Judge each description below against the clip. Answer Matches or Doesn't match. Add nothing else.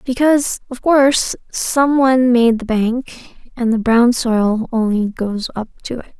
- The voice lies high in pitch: Matches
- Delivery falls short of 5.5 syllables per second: Matches